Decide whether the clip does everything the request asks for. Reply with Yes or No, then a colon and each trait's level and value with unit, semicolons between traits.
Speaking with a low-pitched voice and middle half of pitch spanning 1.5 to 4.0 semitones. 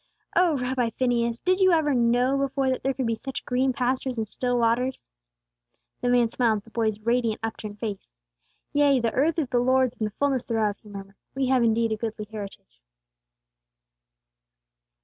No: high, 245 Hz; average, 2.9 semitones